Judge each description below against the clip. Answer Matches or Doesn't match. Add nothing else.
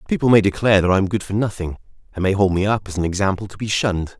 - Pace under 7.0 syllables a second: Doesn't match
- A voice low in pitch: Matches